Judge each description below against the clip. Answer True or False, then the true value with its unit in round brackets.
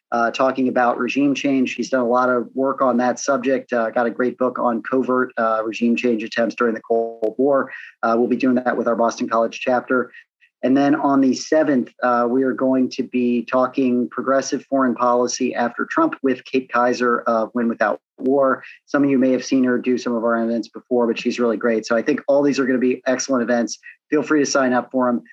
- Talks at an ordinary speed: False (235 wpm)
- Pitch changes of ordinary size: False (1.8 semitones)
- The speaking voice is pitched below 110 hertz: False (125 Hz)